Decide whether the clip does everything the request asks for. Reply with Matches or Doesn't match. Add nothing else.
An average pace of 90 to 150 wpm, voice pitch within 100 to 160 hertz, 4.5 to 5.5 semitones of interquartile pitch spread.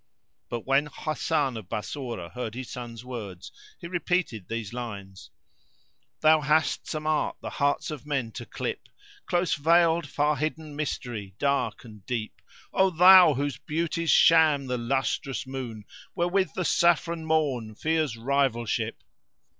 Matches